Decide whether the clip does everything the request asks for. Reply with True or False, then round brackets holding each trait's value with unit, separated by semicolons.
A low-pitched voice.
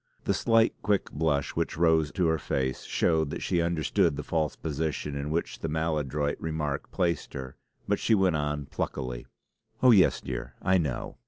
True (80 Hz)